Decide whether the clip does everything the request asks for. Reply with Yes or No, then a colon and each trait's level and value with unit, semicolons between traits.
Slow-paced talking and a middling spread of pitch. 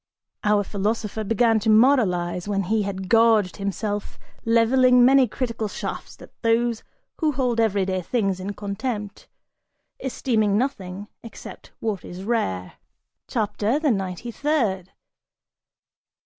Yes: slow, 120 wpm; average, 3.2 semitones